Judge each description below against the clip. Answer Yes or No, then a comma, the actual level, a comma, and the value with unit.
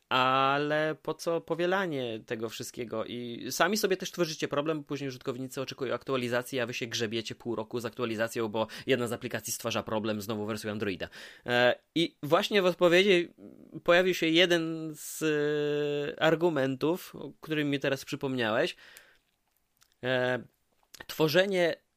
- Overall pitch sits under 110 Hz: No, low, 135 Hz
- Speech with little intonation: No, average, 5.2 semitones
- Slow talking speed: No, average, 130 wpm